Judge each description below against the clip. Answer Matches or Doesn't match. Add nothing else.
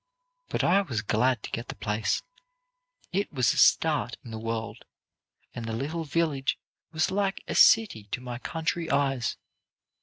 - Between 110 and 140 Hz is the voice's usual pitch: Matches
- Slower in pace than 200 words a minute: Matches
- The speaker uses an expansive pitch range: Matches